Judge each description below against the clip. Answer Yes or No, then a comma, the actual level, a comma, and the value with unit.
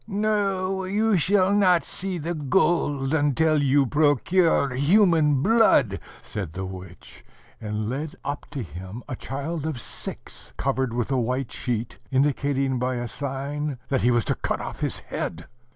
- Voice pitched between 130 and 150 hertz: Yes, medium, 140 Hz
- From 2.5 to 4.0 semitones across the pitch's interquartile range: No, wide, 5.4 semitones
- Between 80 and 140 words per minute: No, average, 155 wpm